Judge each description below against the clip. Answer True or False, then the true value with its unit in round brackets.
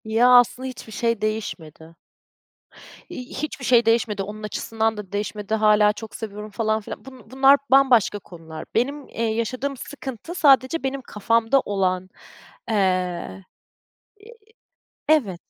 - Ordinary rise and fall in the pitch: True (3.9 semitones)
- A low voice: False (220 Hz)